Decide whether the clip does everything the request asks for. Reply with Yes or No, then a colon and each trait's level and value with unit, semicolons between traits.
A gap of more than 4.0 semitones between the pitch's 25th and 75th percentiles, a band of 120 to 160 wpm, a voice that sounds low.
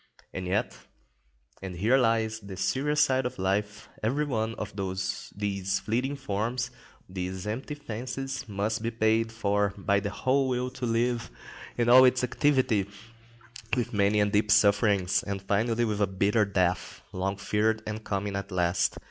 No: average, 3.3 semitones; average, 155 wpm; low, 105 Hz